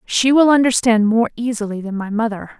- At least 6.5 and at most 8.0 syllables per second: No, 5.4 syllables/s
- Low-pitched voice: No, high, 230 Hz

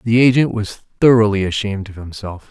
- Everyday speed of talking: Yes, average, 170 wpm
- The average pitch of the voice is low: Yes, low, 105 Hz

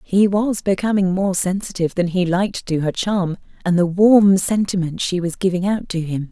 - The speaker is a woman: Yes, female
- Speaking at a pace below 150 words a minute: No, average, 200 wpm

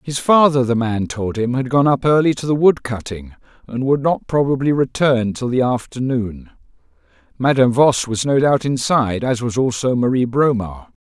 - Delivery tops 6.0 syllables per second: No, 4.9 syllables/s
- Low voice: Yes, low, 125 Hz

